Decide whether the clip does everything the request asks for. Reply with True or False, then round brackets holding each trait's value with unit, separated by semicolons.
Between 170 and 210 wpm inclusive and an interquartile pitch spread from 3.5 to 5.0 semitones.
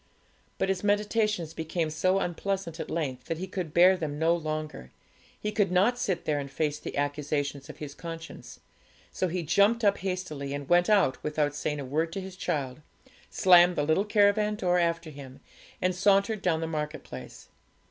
True (180 wpm; 4.2 semitones)